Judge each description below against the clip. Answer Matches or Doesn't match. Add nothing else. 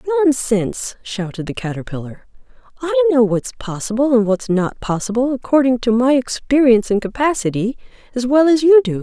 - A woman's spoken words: Matches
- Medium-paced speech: Matches